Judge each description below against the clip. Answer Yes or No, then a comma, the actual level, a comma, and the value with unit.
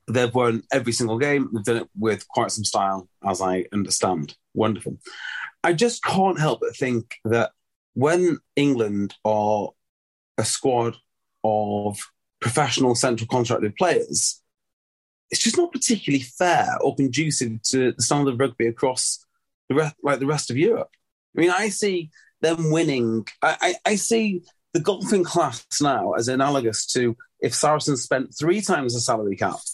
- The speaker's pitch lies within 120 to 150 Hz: Yes, low, 135 Hz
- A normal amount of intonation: No, wide, 6.7 semitones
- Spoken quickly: No, average, 155 wpm